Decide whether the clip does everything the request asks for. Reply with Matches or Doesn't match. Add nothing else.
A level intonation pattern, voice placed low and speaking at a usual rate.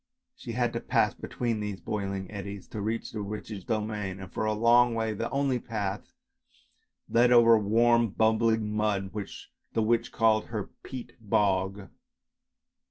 Matches